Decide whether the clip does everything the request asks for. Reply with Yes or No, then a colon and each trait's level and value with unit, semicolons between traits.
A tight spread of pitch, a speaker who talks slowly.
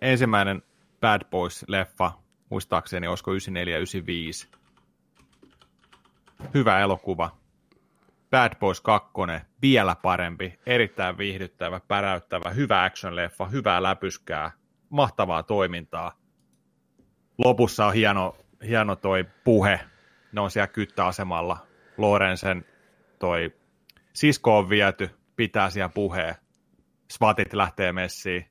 Yes: narrow, 2.3 semitones; slow, 90 wpm